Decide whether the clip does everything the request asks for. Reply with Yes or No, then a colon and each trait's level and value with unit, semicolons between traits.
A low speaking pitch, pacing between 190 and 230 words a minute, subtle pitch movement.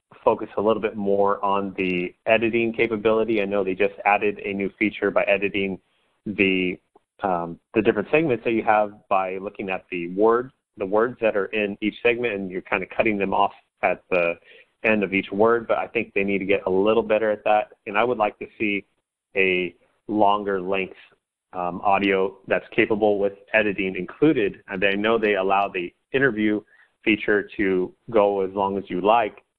Yes: low, 100 Hz; average, 195 wpm; narrow, 2.0 semitones